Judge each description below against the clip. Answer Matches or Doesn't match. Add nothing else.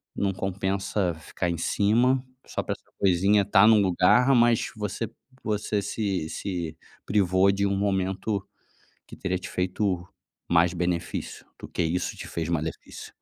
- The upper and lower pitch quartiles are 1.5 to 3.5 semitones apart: Matches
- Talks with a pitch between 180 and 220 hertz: Doesn't match